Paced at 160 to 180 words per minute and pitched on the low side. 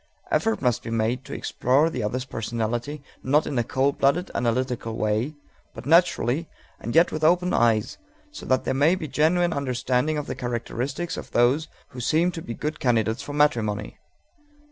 Yes: average, 175 wpm; low, 130 Hz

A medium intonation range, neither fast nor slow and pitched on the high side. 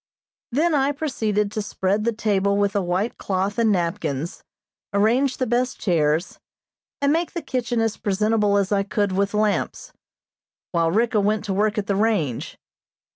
Yes: average, 3.0 semitones; average, 165 wpm; high, 210 Hz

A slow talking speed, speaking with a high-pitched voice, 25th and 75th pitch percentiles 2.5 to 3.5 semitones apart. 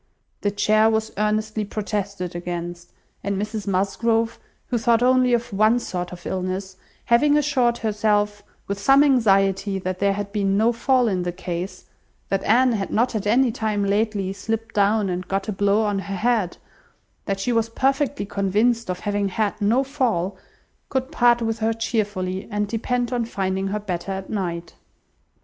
No: average, 170 wpm; high, 210 Hz; average, 3.0 semitones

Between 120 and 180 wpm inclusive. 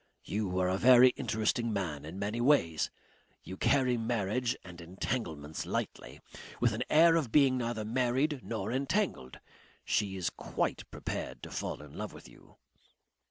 Yes: average, 155 wpm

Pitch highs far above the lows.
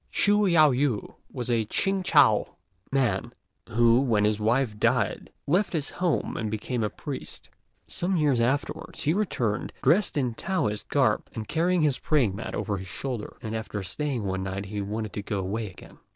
Yes: wide, 6.1 semitones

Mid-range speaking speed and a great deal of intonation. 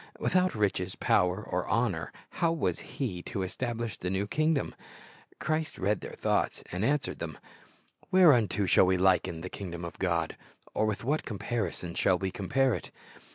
Yes: average, 165 wpm; wide, 6.5 semitones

